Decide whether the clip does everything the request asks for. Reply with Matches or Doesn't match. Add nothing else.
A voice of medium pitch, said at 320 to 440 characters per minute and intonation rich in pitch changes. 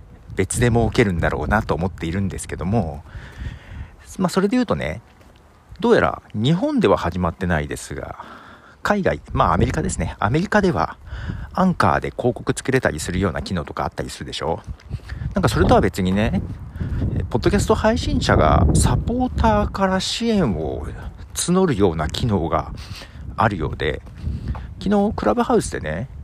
Doesn't match